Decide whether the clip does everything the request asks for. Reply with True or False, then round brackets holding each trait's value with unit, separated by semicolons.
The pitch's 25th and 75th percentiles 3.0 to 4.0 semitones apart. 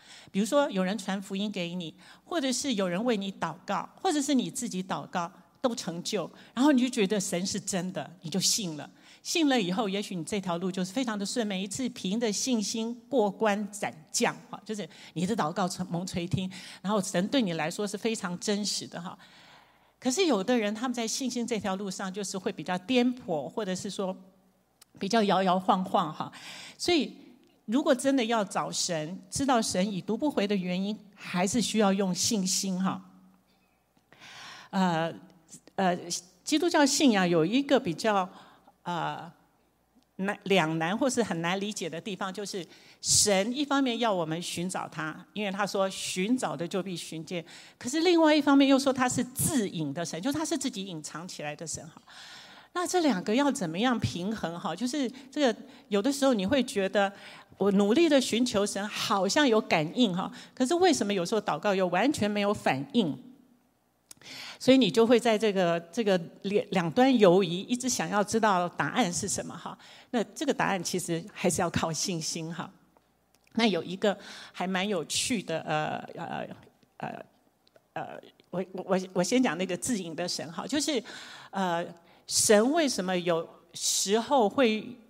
False (5.3 semitones)